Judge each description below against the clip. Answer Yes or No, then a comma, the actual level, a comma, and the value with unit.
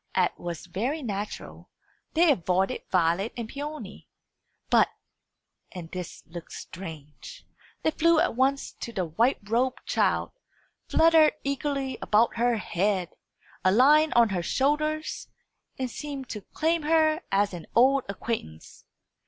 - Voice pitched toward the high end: Yes, high, 235 Hz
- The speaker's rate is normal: No, slow, 130 wpm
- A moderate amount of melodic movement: No, wide, 7.9 semitones